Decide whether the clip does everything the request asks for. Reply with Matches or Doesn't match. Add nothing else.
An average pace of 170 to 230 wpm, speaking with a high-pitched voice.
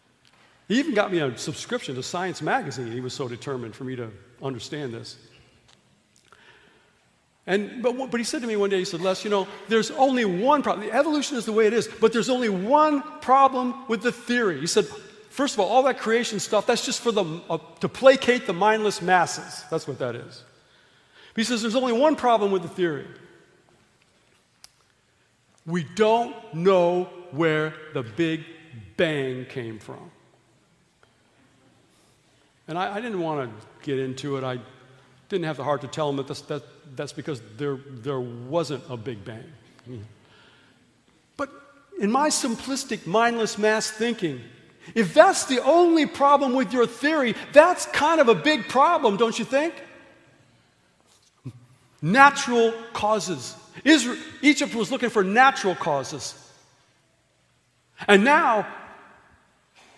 Doesn't match